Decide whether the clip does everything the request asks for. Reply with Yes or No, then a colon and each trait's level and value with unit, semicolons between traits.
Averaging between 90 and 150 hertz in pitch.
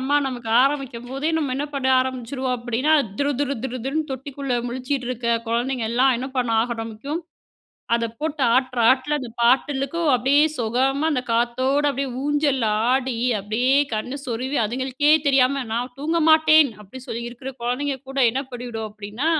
No: very high, 260 Hz